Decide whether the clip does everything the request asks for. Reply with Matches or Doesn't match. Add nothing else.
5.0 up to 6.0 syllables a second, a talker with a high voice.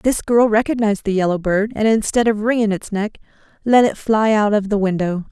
Matches